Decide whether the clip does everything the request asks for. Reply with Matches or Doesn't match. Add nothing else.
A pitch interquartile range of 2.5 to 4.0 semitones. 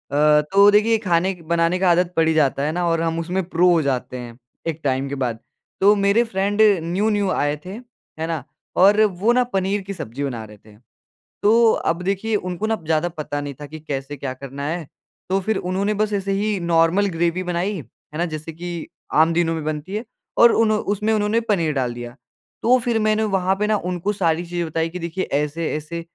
Doesn't match